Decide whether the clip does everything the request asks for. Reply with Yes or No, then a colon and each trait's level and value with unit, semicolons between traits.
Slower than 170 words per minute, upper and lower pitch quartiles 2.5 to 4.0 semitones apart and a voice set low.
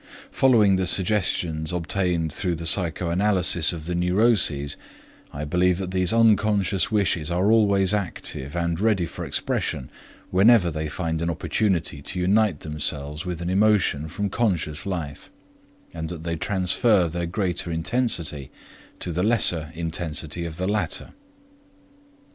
Yes: slow, 135 wpm; average, 3.6 semitones; very low, 90 Hz